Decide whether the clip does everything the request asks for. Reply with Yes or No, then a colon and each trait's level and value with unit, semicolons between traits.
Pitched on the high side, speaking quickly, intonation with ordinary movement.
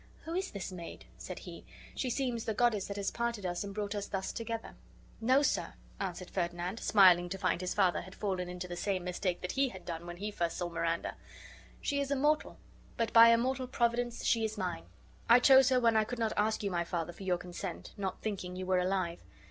Yes: high, 200 Hz; fast, 225 wpm; average, 4.5 semitones